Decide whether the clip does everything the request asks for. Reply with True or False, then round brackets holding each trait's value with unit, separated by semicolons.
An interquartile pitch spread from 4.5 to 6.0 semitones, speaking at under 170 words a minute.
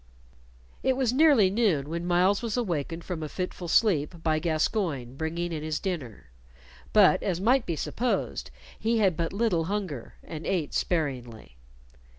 True (5.0 semitones; 155 wpm)